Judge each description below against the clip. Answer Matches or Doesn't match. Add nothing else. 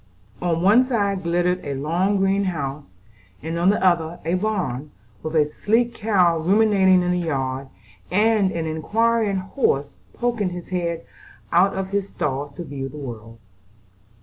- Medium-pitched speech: Matches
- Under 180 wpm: Matches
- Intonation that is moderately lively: Matches